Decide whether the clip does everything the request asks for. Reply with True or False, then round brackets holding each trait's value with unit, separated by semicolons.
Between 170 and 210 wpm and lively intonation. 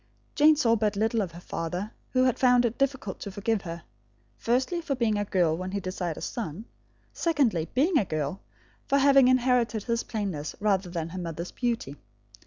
True (190 wpm; 5.9 semitones)